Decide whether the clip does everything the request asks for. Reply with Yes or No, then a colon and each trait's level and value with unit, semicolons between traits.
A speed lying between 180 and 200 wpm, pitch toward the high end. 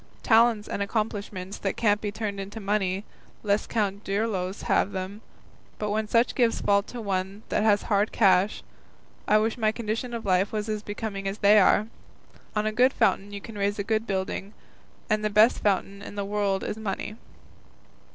Yes: average, 185 wpm; high, 205 Hz